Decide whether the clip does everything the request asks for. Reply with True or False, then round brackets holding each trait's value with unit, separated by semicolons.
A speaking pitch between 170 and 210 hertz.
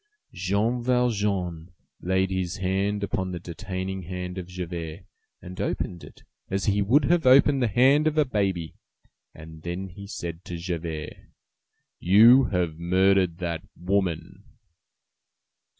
False (95 Hz)